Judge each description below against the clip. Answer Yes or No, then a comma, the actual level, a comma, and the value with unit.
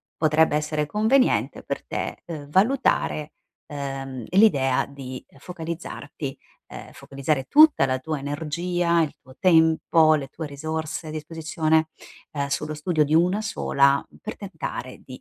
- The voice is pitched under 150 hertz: No, medium, 155 Hz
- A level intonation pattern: No, average, 3.2 semitones